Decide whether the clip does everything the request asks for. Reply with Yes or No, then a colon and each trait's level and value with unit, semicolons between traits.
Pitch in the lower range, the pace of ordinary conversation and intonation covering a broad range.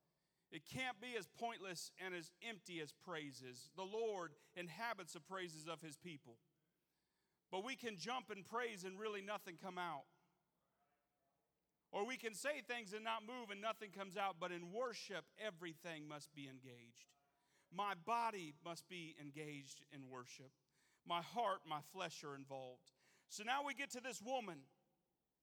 No: medium, 180 Hz; average, 160 wpm; wide, 6.1 semitones